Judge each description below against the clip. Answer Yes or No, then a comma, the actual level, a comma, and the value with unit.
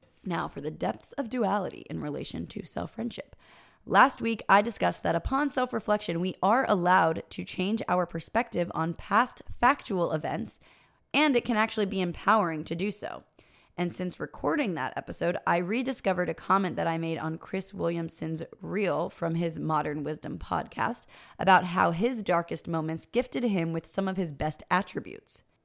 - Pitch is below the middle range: No, medium, 185 Hz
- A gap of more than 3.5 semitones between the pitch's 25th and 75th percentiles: Yes, average, 5.2 semitones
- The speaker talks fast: No, average, 170 wpm